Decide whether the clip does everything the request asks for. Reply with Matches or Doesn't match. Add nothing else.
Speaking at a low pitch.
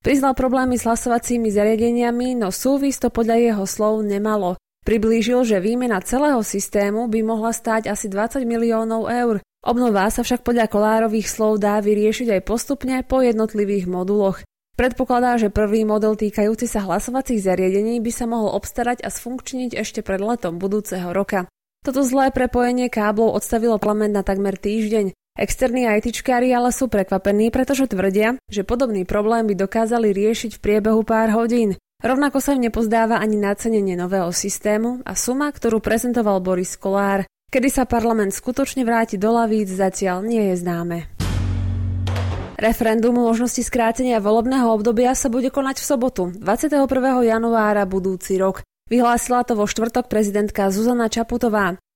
Doesn't match